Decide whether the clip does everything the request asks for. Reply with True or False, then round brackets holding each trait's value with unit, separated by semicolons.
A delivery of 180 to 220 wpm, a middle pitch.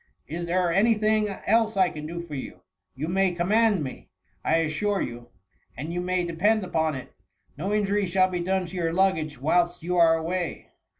True (190 wpm; 175 Hz)